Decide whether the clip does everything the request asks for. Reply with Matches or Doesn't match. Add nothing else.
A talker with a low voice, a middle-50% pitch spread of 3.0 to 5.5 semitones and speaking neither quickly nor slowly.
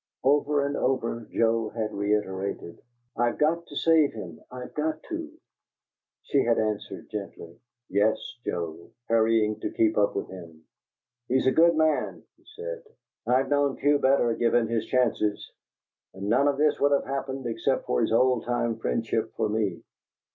Matches